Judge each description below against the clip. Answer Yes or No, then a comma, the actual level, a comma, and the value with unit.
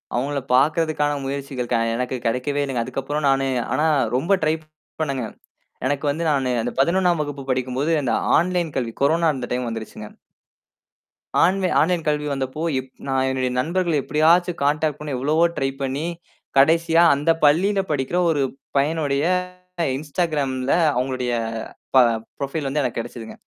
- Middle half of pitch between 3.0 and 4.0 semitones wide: Yes, average, 3.3 semitones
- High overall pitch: No, medium, 145 Hz